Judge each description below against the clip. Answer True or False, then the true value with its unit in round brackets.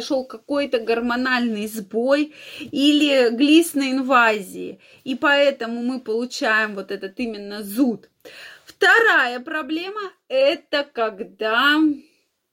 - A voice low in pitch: False (260 Hz)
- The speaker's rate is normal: False (85 wpm)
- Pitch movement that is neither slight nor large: True (4.1 semitones)